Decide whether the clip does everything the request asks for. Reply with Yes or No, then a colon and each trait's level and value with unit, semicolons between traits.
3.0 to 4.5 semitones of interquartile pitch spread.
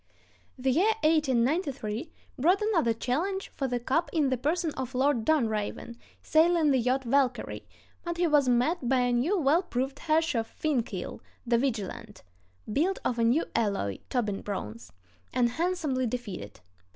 No: average, 5.2 semitones